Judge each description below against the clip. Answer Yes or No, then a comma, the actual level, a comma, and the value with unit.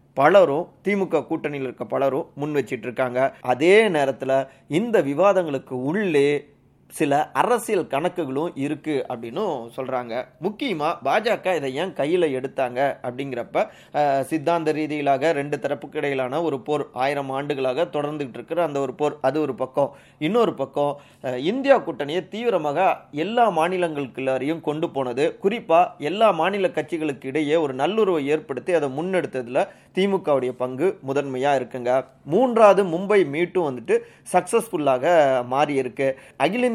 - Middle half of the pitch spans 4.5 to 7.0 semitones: No, average, 4.1 semitones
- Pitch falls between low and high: Yes, medium, 145 Hz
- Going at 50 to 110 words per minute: No, average, 120 wpm